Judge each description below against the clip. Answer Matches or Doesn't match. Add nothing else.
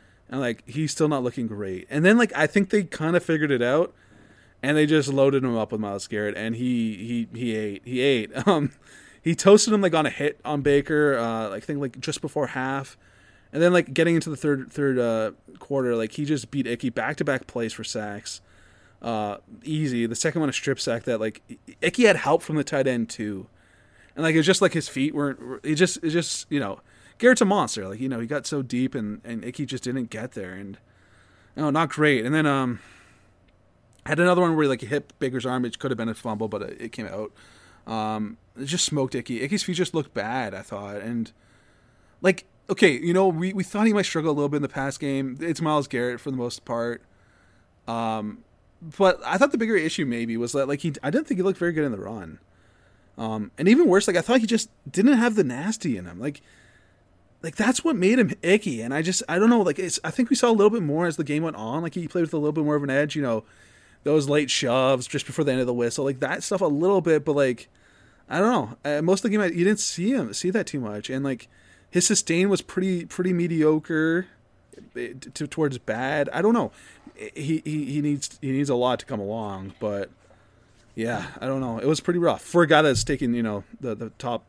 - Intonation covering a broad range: Matches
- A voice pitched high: Doesn't match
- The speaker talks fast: Matches